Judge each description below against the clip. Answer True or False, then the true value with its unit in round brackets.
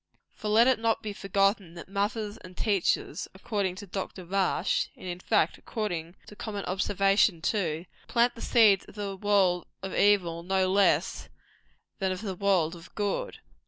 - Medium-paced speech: True (165 wpm)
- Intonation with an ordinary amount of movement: False (2.3 semitones)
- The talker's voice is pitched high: True (195 Hz)